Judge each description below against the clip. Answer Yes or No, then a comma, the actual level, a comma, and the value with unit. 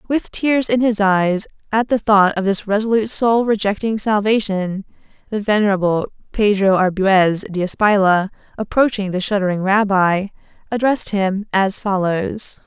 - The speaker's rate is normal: No, slow, 130 wpm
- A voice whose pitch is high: Yes, high, 205 Hz